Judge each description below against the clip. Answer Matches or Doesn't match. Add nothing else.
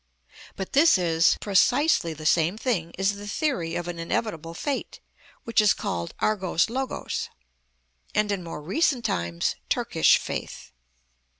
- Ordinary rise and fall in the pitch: Doesn't match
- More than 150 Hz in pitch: Matches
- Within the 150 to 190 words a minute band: Doesn't match